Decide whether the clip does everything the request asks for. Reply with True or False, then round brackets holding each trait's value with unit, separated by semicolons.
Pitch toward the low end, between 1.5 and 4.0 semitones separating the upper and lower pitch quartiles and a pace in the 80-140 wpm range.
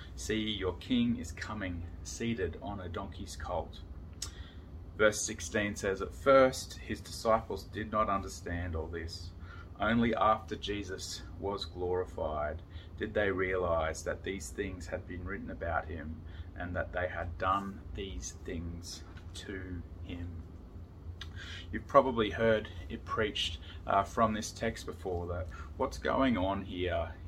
True (90 Hz; 3.2 semitones; 135 wpm)